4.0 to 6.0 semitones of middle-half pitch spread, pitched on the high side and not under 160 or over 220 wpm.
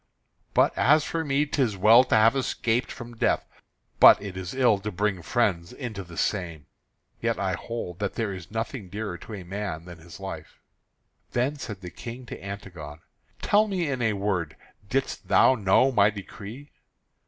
No: average, 4.6 semitones; low, 105 Hz; average, 175 wpm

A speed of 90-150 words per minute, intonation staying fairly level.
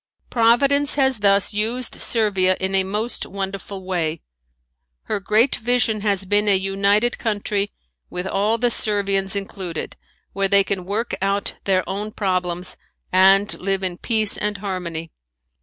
Yes: average, 140 wpm; narrow, 2.0 semitones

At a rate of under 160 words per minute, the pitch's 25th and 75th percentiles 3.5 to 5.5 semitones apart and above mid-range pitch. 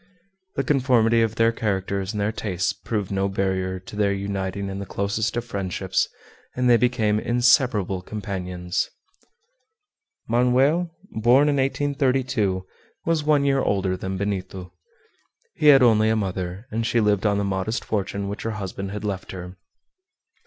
No: average, 150 wpm; average, 3.9 semitones; low, 105 Hz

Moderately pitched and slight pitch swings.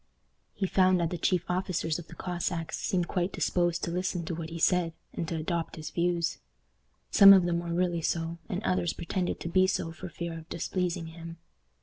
Yes: medium, 170 Hz; narrow, 1.5 semitones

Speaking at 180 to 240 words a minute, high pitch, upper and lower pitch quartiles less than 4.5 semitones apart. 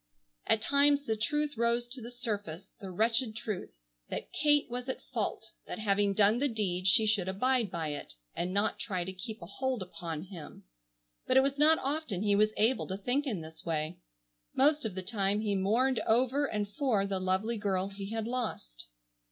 No: average, 195 wpm; high, 215 Hz; average, 4.9 semitones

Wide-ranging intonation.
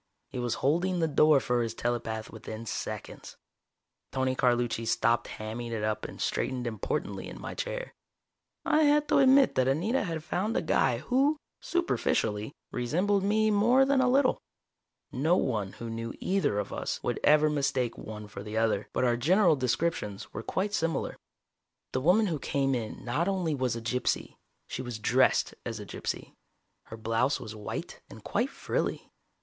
Yes: wide, 8.6 semitones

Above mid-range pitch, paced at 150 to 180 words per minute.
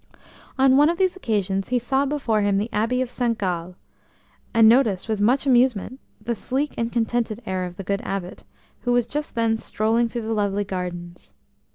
No: high, 225 Hz; average, 190 wpm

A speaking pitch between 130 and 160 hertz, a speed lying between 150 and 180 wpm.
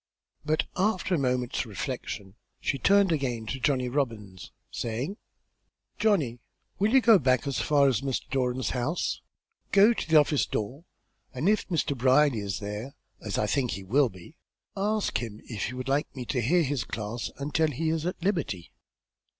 Yes: low, 135 Hz; average, 175 wpm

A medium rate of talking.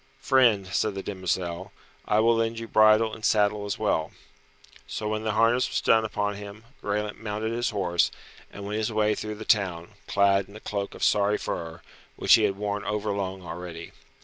Yes: average, 190 wpm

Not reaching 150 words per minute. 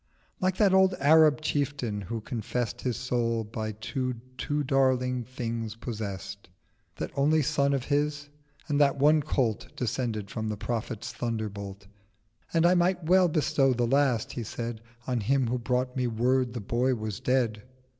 No: average, 165 wpm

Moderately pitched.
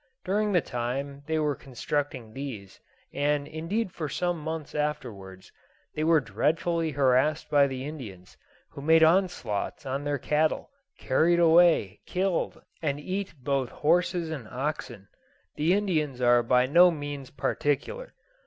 Yes: medium, 150 Hz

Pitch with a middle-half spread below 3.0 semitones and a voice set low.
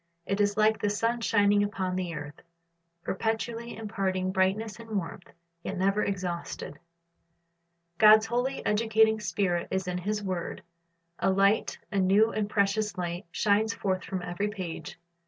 No: narrow, 2.6 semitones; high, 200 Hz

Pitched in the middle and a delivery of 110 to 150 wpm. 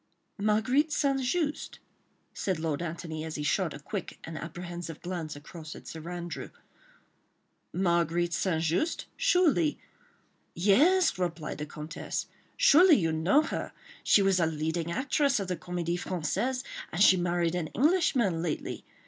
Yes: medium, 175 Hz; average, 140 wpm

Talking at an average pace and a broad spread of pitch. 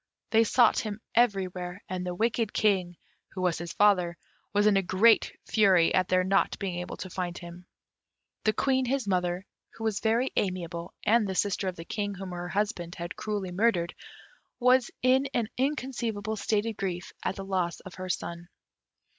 No: average, 180 wpm; average, 3.6 semitones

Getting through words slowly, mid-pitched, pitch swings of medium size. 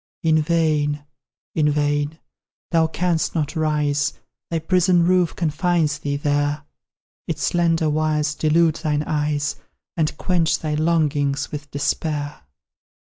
No: slow, 120 wpm; medium, 155 Hz; narrow, 1.9 semitones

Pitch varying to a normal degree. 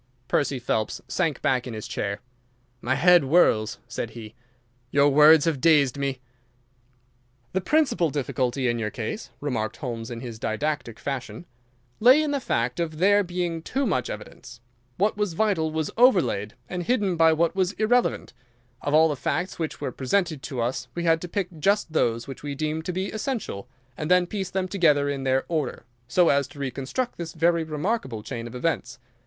No: wide, 6.0 semitones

